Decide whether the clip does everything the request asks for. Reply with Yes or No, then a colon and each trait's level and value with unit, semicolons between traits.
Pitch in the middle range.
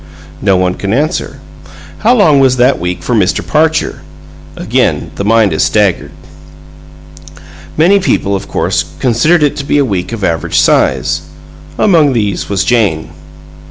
No: low, 115 Hz